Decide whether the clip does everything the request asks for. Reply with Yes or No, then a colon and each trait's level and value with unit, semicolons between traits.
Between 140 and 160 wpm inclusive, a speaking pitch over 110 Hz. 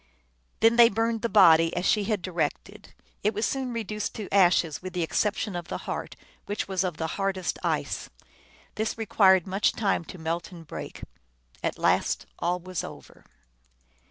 No: average, 175 wpm; high, 190 Hz